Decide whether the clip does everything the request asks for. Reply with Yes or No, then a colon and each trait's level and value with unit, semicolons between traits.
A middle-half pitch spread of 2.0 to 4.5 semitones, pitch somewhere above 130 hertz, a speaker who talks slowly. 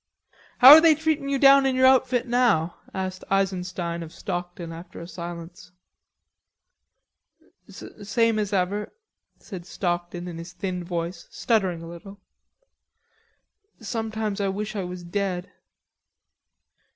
Yes: average, 4.2 semitones; high, 190 Hz; slow, 125 wpm